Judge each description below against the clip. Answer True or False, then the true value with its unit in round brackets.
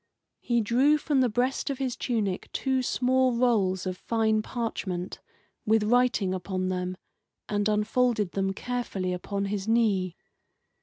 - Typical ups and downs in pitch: True (4.5 semitones)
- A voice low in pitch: False (215 Hz)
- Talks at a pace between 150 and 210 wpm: False (140 wpm)